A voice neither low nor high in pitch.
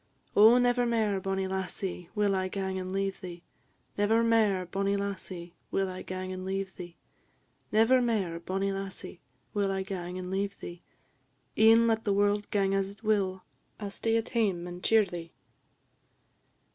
No: high, 195 Hz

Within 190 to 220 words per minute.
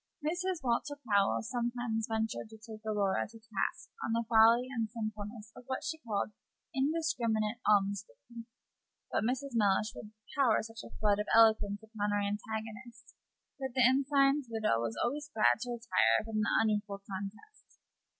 No: average, 155 wpm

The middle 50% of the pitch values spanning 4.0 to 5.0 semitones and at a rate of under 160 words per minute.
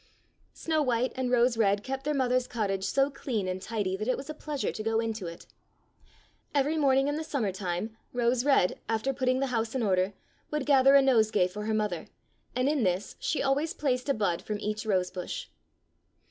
No: average, 4.7 semitones; average, 200 wpm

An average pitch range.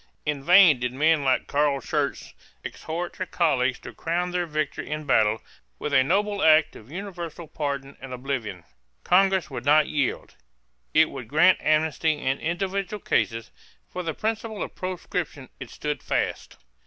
Yes: average, 4.6 semitones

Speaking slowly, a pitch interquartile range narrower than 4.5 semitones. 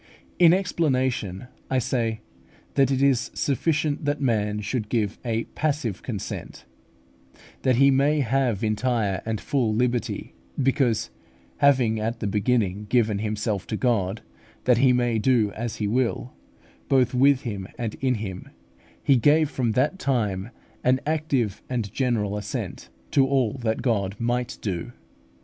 No: average, 145 wpm; average, 3.8 semitones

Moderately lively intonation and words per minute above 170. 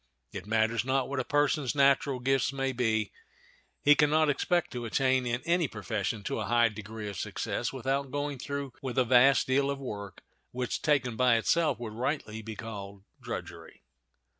Yes: average, 3.8 semitones; average, 180 wpm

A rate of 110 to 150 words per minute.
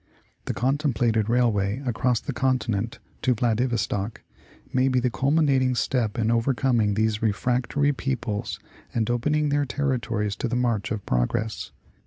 Yes: average, 140 wpm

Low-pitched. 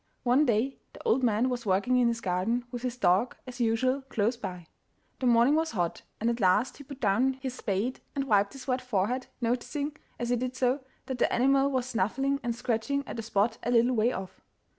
No: high, 245 Hz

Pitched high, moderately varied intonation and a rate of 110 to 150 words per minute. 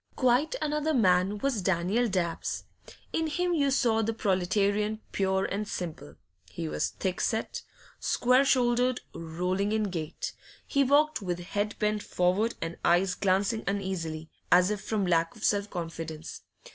Yes: high, 200 Hz; average, 4.8 semitones; average, 145 wpm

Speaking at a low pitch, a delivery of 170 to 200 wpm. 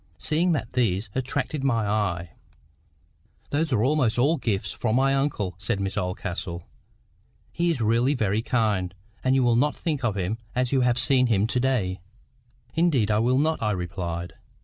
Yes: low, 120 Hz; average, 175 wpm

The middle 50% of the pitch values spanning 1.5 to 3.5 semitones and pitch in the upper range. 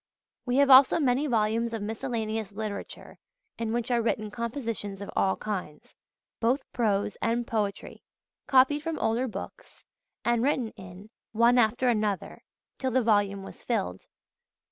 Yes: average, 2.9 semitones; high, 225 Hz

